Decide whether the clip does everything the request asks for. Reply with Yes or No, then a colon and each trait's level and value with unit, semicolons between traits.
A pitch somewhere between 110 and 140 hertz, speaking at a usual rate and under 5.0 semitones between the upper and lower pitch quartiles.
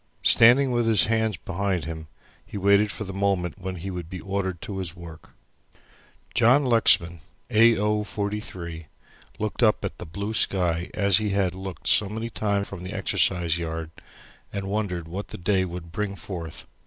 No: very low, 95 Hz; average, 175 wpm; average, 3.3 semitones